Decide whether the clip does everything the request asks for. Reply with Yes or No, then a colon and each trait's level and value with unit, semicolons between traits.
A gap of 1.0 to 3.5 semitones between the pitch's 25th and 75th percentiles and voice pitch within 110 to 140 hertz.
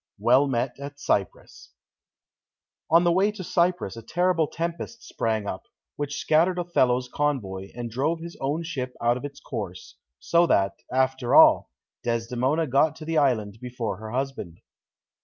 No: wide, 5.6 semitones; low, 135 Hz